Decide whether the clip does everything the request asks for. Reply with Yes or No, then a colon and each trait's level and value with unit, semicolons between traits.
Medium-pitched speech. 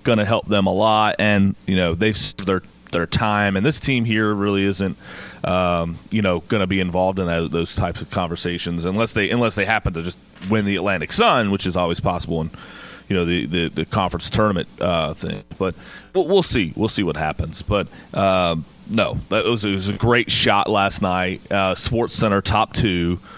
No: low, 100 Hz